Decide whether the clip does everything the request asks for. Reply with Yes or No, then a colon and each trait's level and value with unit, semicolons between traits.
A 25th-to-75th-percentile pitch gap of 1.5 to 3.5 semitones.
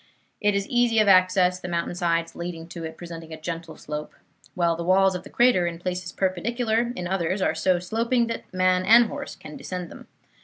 Yes: average, 2.8 semitones